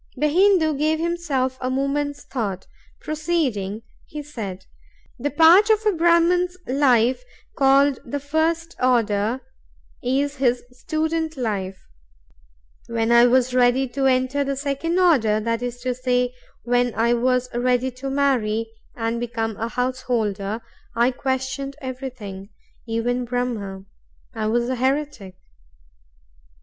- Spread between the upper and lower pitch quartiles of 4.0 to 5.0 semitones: No, average, 3.6 semitones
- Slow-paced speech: Yes, slow, 120 wpm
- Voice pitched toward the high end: Yes, very high, 255 Hz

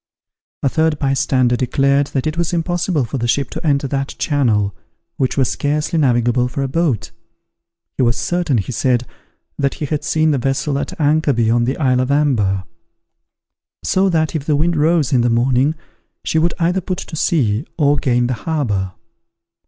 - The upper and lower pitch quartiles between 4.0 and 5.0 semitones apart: Yes, average, 4.3 semitones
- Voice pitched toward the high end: No, medium, 140 Hz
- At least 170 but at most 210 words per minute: Yes, average, 180 wpm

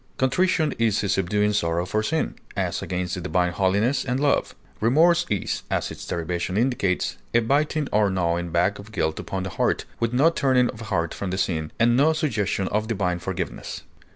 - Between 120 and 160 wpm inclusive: No, average, 185 wpm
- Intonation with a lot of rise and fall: Yes, wide, 5.7 semitones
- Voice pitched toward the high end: No, low, 105 Hz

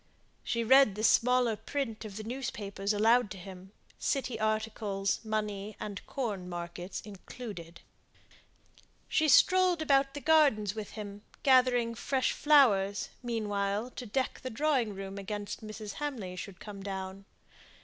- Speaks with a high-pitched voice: Yes, high, 215 Hz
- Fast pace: No, slow, 135 wpm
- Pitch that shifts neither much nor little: Yes, average, 4.2 semitones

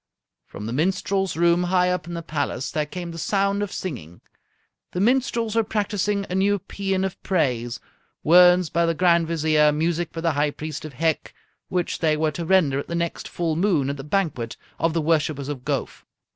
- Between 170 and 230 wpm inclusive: Yes, average, 200 wpm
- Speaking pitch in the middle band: Yes, medium, 170 Hz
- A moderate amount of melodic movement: Yes, average, 3.7 semitones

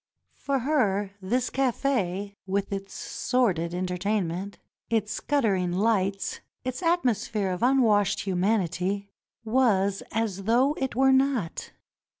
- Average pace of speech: No, slow, 115 wpm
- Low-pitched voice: No, high, 205 Hz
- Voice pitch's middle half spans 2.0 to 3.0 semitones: No, average, 4.7 semitones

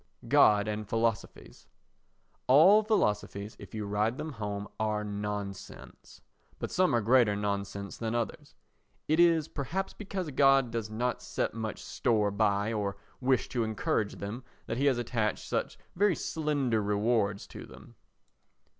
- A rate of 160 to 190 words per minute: No, average, 145 wpm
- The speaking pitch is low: Yes, low, 110 Hz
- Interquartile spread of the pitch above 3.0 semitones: Yes, average, 4.5 semitones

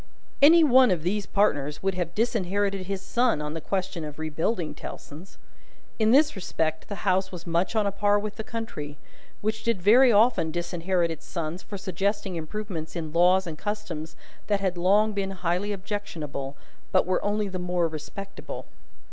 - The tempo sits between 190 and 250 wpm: No, average, 175 wpm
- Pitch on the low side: No, high, 190 Hz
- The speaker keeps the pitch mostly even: No, average, 3.8 semitones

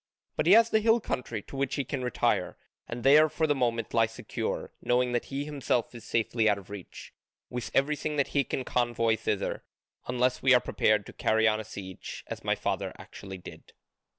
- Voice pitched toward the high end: No, low, 125 Hz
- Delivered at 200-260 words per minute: Yes, fast, 205 wpm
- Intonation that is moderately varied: Yes, average, 3.9 semitones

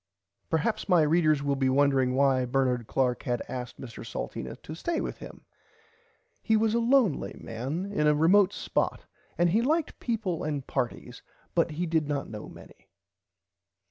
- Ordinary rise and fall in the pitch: No, wide, 6.5 semitones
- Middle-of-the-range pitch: Yes, medium, 150 Hz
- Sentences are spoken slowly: No, average, 165 wpm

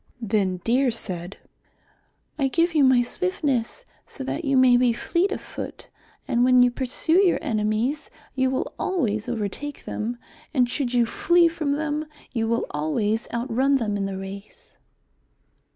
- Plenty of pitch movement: No, average, 4.9 semitones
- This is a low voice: No, very high, 250 Hz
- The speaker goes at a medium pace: Yes, average, 160 wpm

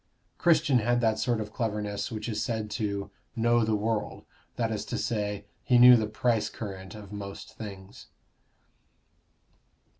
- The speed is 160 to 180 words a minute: No, average, 150 wpm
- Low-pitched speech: Yes, low, 110 Hz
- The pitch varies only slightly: Yes, narrow, 2.3 semitones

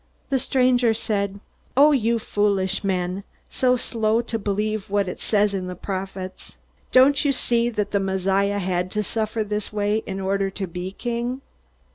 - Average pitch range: Yes, average, 3.3 semitones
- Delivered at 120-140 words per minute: No, average, 165 wpm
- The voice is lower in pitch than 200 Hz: No, high, 205 Hz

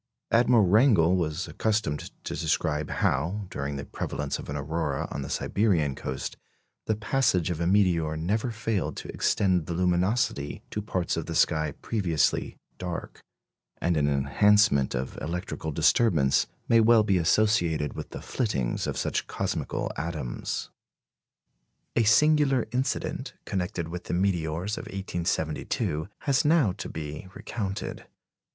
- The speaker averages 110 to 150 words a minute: Yes, average, 140 wpm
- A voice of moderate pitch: No, very low, 90 Hz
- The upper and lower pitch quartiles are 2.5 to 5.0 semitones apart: No, wide, 5.6 semitones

